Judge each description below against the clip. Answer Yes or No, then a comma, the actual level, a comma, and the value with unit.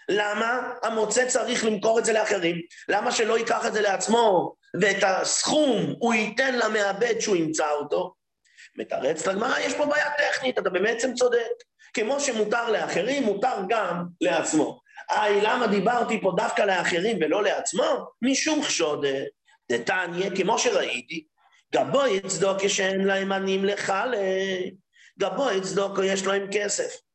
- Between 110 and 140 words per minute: Yes, slow, 135 wpm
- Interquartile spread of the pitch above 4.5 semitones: Yes, average, 4.9 semitones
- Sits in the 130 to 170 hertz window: No, high, 220 Hz